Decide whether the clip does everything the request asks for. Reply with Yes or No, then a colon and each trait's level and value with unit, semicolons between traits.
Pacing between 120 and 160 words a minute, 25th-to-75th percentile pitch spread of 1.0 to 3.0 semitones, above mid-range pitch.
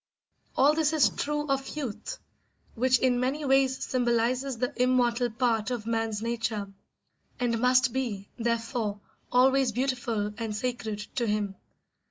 Yes: slow, 135 wpm; narrow, 2.6 semitones; high, 245 Hz